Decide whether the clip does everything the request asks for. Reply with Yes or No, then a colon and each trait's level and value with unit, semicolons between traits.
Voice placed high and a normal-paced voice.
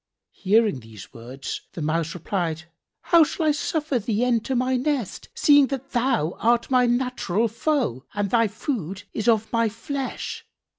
Yes: high, 230 Hz; average, 155 wpm